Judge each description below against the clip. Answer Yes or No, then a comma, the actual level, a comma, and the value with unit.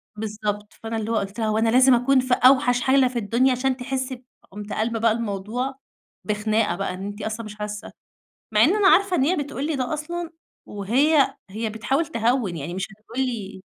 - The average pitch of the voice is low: No, high, 230 Hz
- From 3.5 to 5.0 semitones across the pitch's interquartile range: Yes, average, 4.0 semitones